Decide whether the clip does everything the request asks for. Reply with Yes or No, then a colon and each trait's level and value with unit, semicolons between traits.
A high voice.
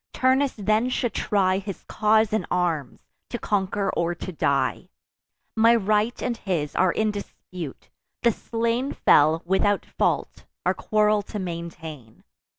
Yes: high, 205 Hz